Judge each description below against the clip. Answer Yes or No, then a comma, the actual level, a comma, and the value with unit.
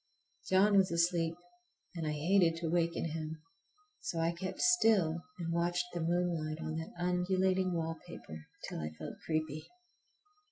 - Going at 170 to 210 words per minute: No, average, 145 wpm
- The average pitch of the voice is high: No, medium, 170 Hz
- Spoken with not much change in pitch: Yes, narrow, 1.8 semitones